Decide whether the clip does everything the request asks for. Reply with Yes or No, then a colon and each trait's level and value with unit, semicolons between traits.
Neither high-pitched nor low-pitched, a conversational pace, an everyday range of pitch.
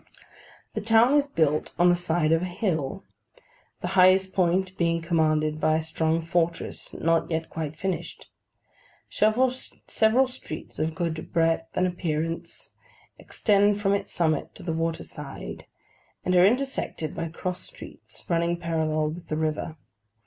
Yes: medium, 170 Hz; average, 145 wpm; average, 3.0 semitones